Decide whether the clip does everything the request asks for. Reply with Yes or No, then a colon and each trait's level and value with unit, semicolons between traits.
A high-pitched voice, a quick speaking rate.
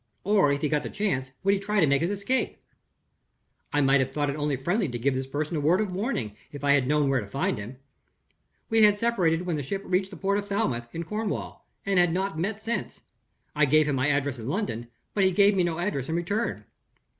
No: medium, 165 Hz; fast, 240 wpm